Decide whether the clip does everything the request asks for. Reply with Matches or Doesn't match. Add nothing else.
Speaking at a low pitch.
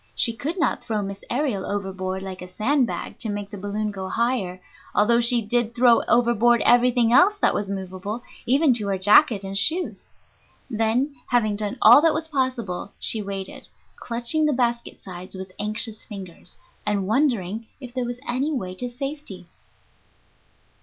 Doesn't match